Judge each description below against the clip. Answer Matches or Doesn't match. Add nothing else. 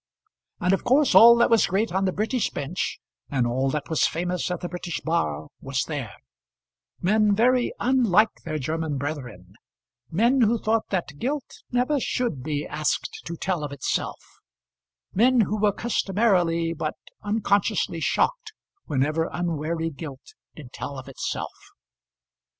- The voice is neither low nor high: Matches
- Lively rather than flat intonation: Matches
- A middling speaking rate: Matches